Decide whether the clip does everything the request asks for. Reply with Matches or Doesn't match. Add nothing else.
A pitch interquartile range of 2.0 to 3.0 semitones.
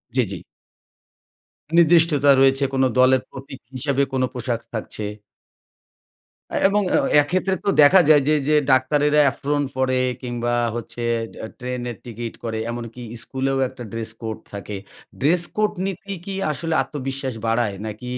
Doesn't match